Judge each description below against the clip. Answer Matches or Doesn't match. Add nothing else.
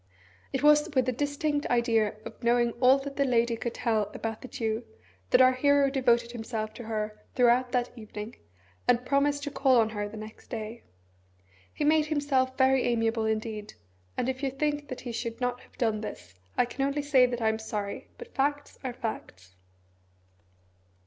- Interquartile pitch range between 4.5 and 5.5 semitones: Doesn't match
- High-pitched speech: Matches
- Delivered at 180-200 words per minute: Matches